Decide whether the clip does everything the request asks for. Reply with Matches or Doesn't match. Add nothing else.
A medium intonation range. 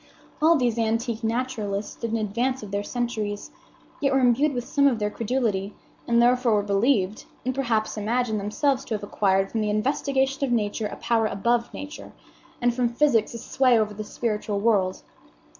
Matches